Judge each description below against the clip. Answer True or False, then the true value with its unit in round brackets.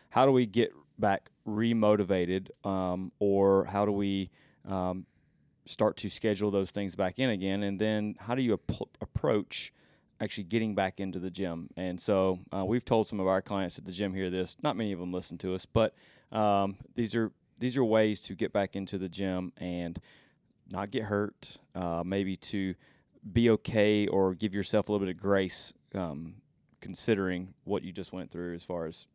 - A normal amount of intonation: False (2.3 semitones)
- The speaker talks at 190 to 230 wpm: True (195 wpm)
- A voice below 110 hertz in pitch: True (100 Hz)